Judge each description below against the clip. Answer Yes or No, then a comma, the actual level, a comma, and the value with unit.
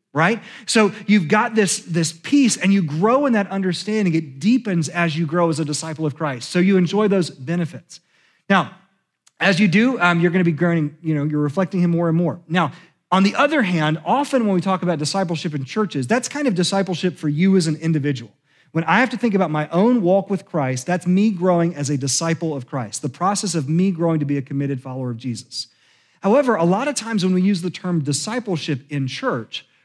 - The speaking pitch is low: No, medium, 175 Hz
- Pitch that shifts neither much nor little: Yes, average, 4.3 semitones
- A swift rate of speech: Yes, fast, 225 wpm